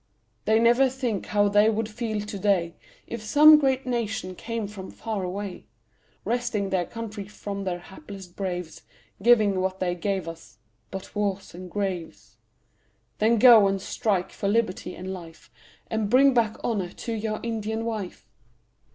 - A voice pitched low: No, high, 205 Hz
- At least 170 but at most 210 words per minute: No, average, 155 wpm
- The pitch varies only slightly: No, average, 3.2 semitones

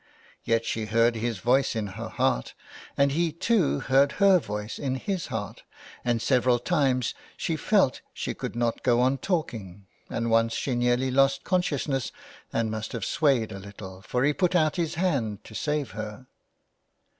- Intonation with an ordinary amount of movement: Yes, average, 4.4 semitones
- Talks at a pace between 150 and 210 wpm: Yes, average, 170 wpm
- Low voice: Yes, low, 125 Hz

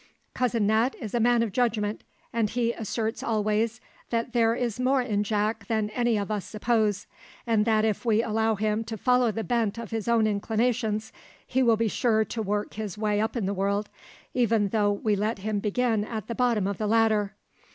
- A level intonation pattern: Yes, narrow, 1.9 semitones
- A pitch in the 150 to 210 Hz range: No, high, 220 Hz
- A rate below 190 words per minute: No, fast, 205 wpm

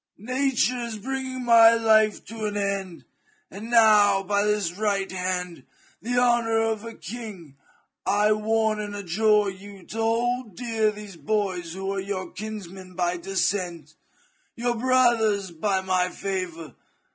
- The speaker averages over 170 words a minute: No, average, 145 wpm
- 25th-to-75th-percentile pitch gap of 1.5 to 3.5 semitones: Yes, average, 3.0 semitones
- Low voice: No, high, 210 Hz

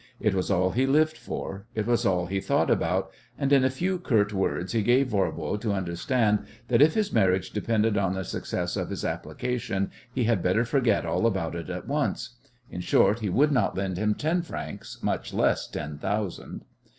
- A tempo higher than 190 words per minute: Yes, average, 200 wpm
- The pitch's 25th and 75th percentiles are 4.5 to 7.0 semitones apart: Yes, average, 4.8 semitones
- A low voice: Yes, low, 105 Hz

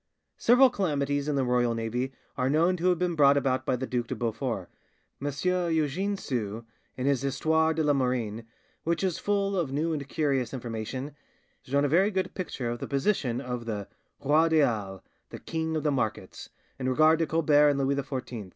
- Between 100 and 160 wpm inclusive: No, average, 195 wpm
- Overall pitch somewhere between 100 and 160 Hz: Yes, medium, 140 Hz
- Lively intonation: No, average, 4.5 semitones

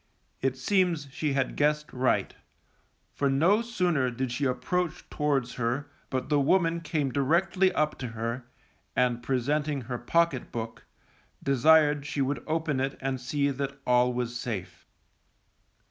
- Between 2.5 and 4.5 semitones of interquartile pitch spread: Yes, average, 3.4 semitones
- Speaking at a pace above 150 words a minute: No, average, 145 wpm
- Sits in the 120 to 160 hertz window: Yes, medium, 140 Hz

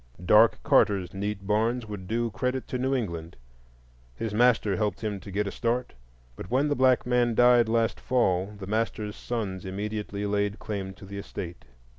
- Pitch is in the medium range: No, low, 105 Hz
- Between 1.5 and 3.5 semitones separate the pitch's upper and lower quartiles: Yes, average, 3.2 semitones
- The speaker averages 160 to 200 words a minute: Yes, average, 175 wpm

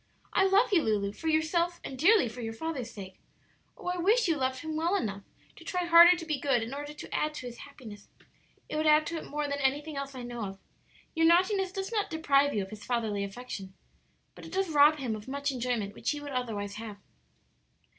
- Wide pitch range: Yes, wide, 6.2 semitones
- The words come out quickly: Yes, fast, 230 wpm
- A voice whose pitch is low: No, very high, 285 Hz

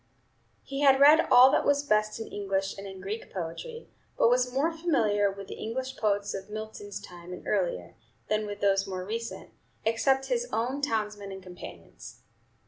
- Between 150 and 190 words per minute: Yes, average, 175 wpm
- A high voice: Yes, high, 215 Hz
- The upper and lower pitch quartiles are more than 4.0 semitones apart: Yes, average, 5.2 semitones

